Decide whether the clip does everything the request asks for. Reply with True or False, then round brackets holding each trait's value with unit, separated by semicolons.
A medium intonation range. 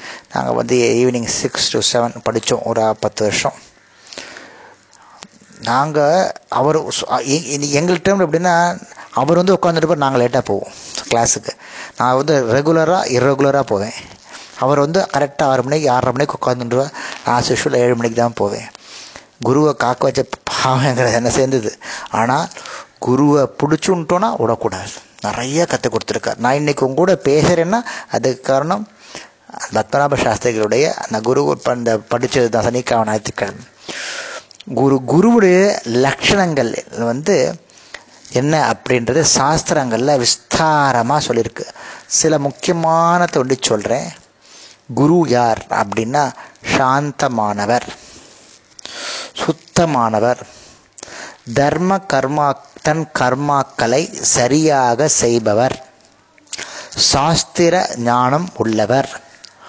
True (4.6 semitones)